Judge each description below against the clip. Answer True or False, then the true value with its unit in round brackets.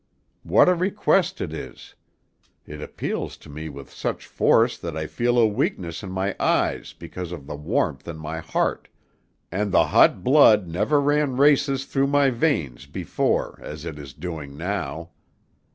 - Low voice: True (90 Hz)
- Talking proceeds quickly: False (165 wpm)